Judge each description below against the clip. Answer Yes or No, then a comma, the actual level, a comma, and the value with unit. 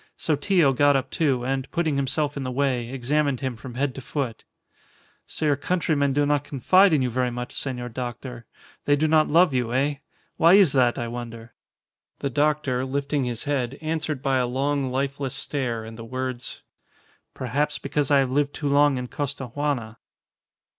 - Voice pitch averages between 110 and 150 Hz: Yes, low, 135 Hz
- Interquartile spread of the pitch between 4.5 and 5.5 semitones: No, average, 2.7 semitones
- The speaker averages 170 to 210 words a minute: Yes, average, 180 wpm